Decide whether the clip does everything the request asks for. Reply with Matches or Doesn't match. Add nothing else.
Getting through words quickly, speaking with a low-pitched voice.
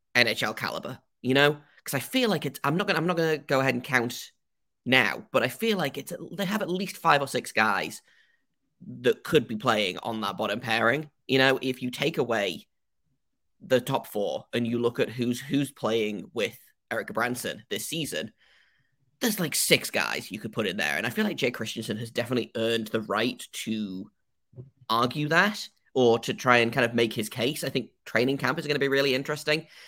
Matches